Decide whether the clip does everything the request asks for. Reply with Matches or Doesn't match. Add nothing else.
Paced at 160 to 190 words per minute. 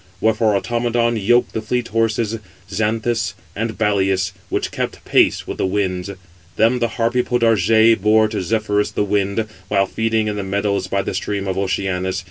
Matches